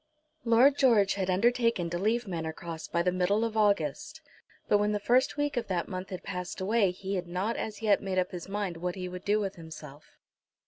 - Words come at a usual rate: No, fast, 220 wpm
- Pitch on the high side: Yes, high, 195 Hz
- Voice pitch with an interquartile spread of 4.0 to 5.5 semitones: No, average, 3.5 semitones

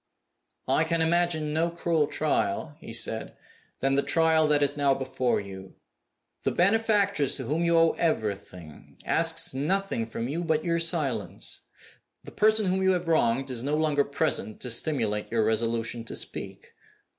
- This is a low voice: No, medium, 150 Hz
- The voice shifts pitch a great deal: Yes, wide, 5.7 semitones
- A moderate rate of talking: Yes, average, 160 wpm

